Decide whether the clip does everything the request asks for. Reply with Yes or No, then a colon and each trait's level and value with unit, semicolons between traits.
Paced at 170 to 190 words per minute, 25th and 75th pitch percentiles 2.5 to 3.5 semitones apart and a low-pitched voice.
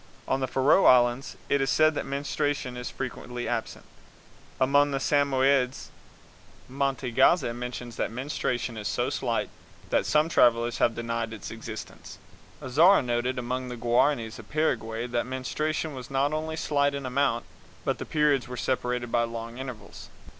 No: average, 155 wpm; average, 2.9 semitones; low, 130 Hz